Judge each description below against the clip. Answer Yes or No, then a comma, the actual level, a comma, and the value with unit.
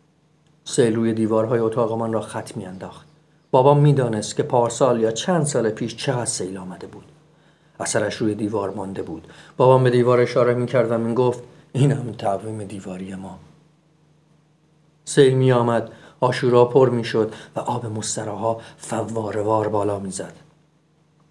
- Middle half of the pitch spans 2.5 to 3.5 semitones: No, average, 4.9 semitones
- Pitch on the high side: No, low, 120 Hz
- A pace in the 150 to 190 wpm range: Yes, fast, 155 wpm